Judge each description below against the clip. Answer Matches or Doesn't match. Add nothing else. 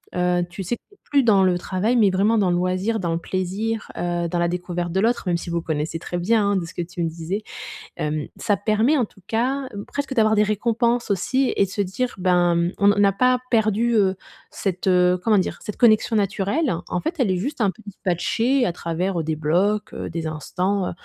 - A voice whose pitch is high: Matches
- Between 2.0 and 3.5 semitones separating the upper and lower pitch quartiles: Doesn't match